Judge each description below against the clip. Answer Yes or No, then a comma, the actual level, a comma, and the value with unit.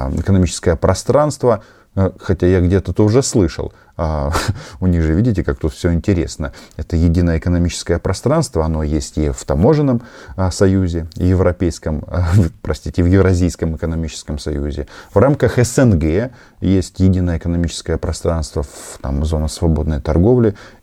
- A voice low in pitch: Yes, very low, 90 Hz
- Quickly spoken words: No, average, 125 wpm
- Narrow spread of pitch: No, average, 3.7 semitones